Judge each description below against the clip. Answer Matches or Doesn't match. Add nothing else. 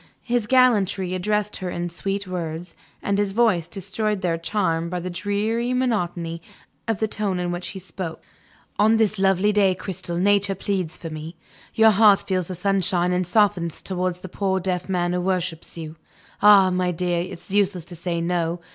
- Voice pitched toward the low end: Doesn't match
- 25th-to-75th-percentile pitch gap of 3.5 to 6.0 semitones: Doesn't match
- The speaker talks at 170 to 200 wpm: Matches